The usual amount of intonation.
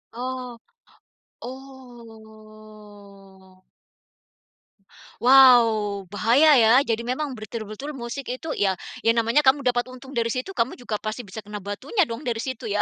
Yes: average, 3.2 semitones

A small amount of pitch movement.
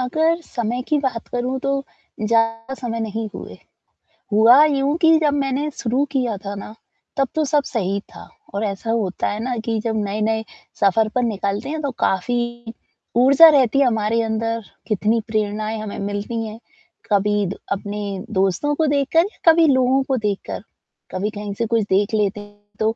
No: average, 4.3 semitones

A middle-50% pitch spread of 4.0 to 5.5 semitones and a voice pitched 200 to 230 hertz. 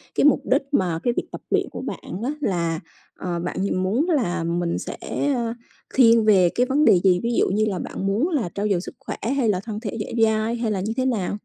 Yes: average, 4.6 semitones; high, 210 Hz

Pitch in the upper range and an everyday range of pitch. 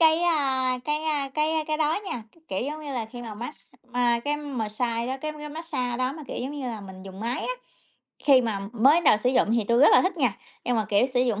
Yes: very high, 255 Hz; average, 4.5 semitones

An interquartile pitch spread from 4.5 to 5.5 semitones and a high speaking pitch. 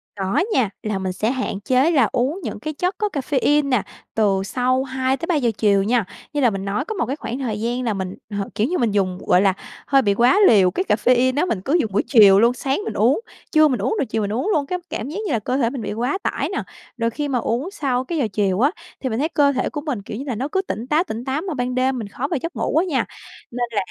Yes: average, 5.1 semitones; very high, 250 Hz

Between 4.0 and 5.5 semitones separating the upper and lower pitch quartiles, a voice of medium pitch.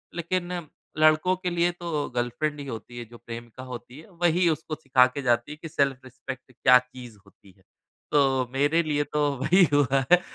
Yes: average, 4.6 semitones; medium, 145 Hz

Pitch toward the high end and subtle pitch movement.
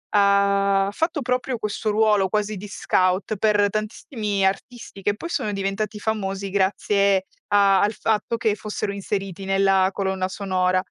Yes: high, 200 Hz; narrow, 1.7 semitones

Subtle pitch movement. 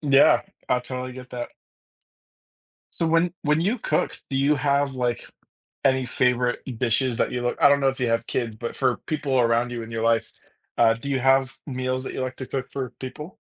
Yes: narrow, 2.2 semitones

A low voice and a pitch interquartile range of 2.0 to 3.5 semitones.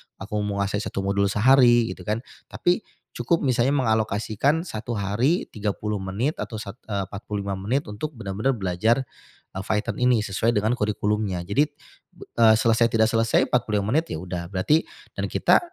Yes: low, 110 Hz; average, 3.2 semitones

